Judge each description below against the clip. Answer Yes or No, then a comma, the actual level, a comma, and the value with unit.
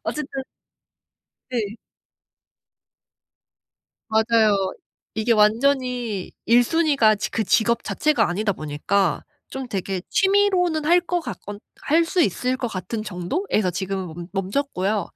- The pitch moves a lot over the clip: Yes, wide, 6.1 semitones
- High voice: Yes, high, 225 Hz